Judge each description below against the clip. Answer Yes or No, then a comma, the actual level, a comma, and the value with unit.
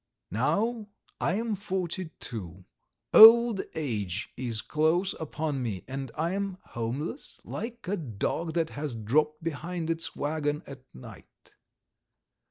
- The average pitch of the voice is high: No, medium, 155 Hz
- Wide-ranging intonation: Yes, wide, 6.3 semitones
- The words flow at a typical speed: No, slow, 125 wpm